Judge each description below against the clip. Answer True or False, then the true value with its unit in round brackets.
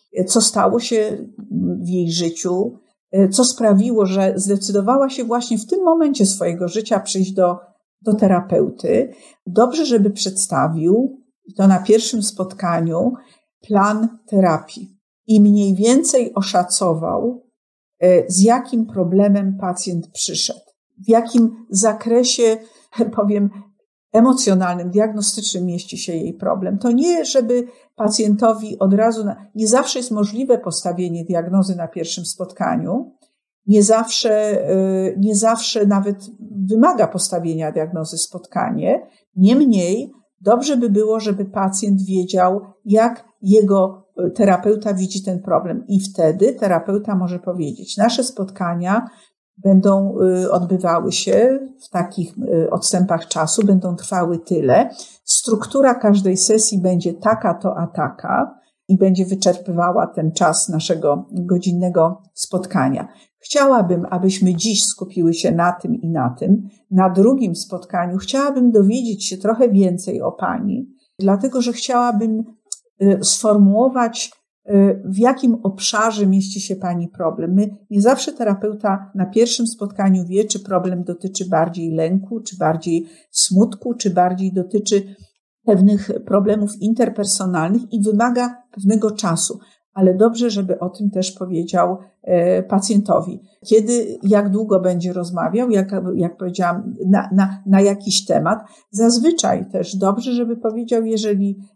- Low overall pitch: False (200 Hz)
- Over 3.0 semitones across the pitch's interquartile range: True (3.5 semitones)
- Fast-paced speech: False (120 wpm)